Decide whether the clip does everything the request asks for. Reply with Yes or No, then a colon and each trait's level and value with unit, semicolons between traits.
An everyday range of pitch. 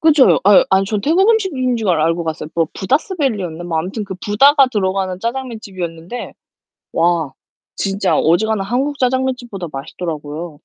No: wide, 7.1 semitones